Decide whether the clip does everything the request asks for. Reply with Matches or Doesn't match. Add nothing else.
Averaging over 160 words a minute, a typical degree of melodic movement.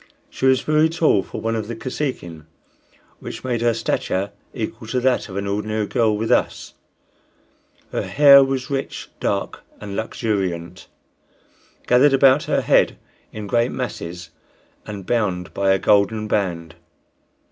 Doesn't match